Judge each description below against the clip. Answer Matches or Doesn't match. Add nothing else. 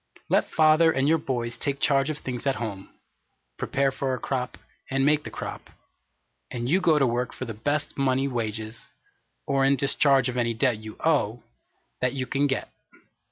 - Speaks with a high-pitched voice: Doesn't match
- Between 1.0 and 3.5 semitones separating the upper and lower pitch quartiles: Matches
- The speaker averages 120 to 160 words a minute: Doesn't match